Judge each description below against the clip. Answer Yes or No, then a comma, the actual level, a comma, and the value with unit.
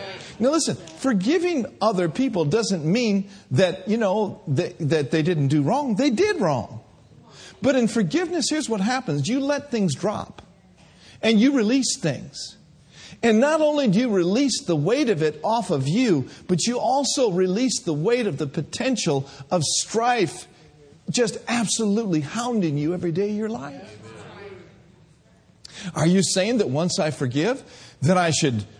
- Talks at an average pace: Yes, average, 165 wpm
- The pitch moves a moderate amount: No, wide, 6.8 semitones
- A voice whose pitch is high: Yes, high, 200 Hz